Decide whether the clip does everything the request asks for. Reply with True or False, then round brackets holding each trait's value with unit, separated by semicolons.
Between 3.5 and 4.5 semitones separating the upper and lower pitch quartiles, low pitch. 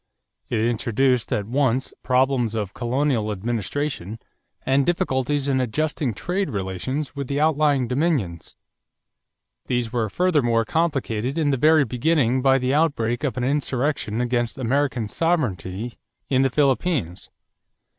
True (3.9 semitones; 130 Hz)